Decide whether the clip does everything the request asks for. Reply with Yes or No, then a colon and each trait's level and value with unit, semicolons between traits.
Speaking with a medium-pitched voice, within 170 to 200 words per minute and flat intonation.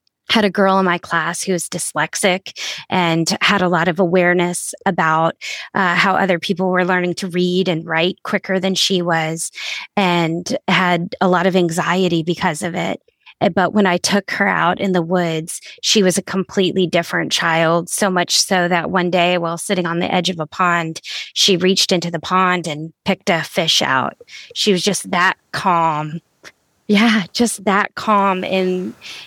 Yes: medium, 180 Hz; average, 180 wpm; narrow, 2.0 semitones